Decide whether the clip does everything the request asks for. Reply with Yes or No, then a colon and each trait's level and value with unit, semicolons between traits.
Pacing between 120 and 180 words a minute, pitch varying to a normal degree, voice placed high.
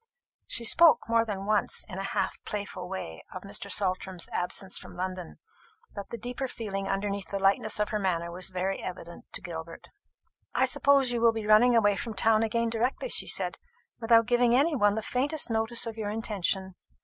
No: average, 190 wpm; average, 3.4 semitones; high, 210 Hz